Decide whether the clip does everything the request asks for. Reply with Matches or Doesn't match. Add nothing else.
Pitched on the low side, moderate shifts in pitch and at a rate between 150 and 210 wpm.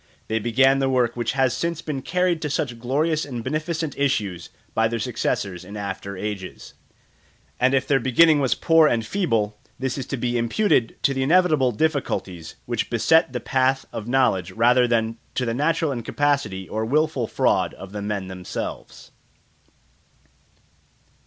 Matches